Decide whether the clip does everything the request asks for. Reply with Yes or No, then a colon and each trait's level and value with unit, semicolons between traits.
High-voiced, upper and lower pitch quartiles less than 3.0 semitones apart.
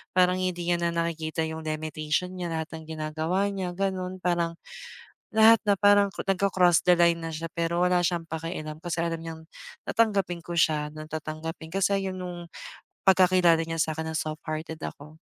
No: medium, 170 Hz; narrow, 2.4 semitones